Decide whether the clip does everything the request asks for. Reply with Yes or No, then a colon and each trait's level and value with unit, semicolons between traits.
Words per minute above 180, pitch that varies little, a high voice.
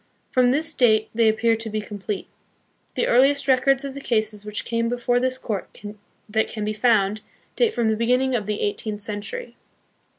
No: average, 190 wpm; average, 3.2 semitones; high, 230 Hz